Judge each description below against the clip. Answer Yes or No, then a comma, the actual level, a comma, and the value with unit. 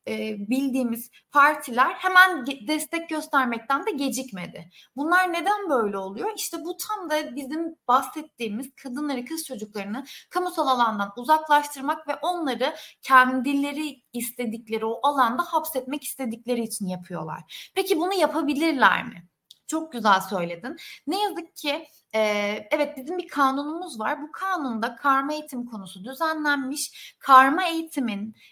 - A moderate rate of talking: Yes, average, 120 wpm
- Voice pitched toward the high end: Yes, very high, 275 Hz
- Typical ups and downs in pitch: Yes, average, 4.9 semitones